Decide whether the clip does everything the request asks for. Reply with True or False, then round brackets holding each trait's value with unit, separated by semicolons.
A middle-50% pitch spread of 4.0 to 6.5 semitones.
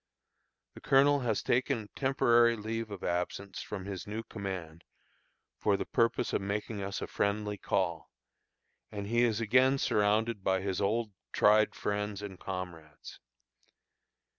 False (2.8 semitones)